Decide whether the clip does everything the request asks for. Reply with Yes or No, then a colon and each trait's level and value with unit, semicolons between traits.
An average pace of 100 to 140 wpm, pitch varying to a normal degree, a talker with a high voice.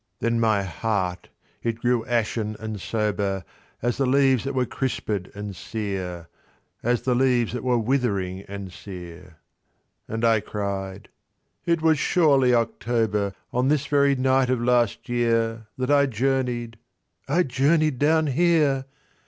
No: slow, 135 wpm; average, 4.5 semitones; low, 120 Hz